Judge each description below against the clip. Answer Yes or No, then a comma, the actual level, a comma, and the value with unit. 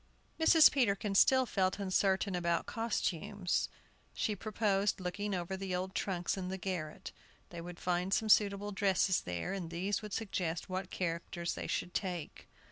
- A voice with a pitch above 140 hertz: Yes, high, 190 Hz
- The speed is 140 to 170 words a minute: Yes, average, 155 wpm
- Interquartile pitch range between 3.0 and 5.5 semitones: No, narrow, 2.5 semitones